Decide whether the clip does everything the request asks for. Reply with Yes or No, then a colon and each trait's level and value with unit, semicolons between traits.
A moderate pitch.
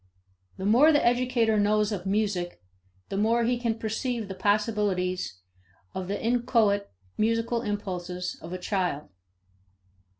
No: high, 210 Hz